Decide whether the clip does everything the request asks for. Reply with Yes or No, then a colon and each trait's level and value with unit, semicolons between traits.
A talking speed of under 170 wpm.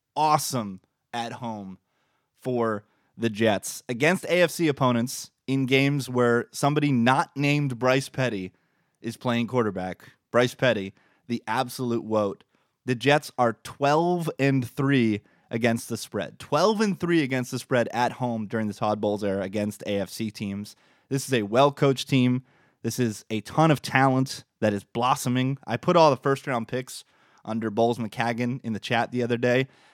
Yes: average, 160 wpm